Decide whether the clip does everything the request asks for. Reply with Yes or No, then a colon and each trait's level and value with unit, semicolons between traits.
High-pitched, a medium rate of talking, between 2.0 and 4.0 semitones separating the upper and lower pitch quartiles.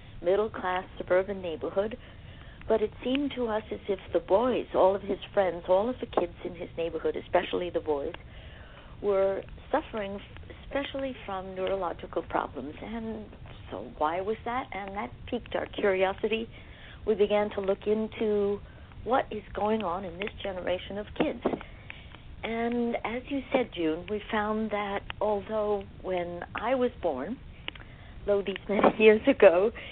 Yes: high, 205 Hz; average, 150 wpm; average, 3.0 semitones